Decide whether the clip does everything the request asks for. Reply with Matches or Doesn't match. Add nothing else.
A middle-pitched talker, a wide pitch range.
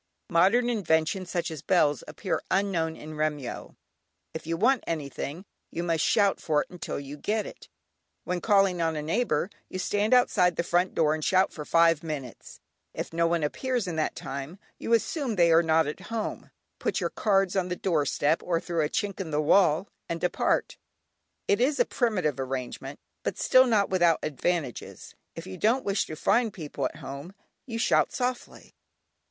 Doesn't match